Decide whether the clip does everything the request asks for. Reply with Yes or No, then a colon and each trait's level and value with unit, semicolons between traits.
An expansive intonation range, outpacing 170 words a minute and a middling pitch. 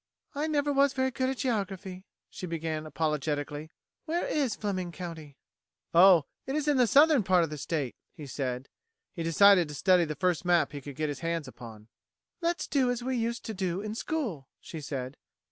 Yes: wide, 8.4 semitones; average, 195 wpm; medium, 180 Hz